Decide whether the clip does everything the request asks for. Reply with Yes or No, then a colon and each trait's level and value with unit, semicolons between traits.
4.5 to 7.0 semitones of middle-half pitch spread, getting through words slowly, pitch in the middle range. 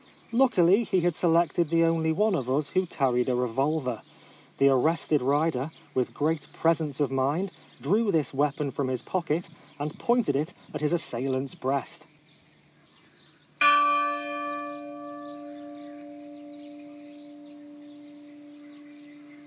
No: average, 3.8 semitones; slow, 105 wpm; medium, 150 Hz